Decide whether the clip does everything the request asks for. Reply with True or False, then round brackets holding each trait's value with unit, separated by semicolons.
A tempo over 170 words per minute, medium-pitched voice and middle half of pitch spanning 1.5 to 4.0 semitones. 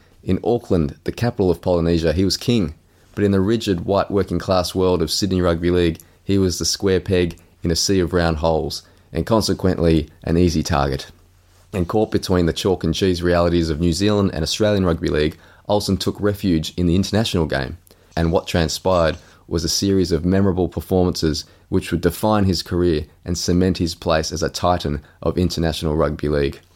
False (190 wpm; 90 Hz; 2.6 semitones)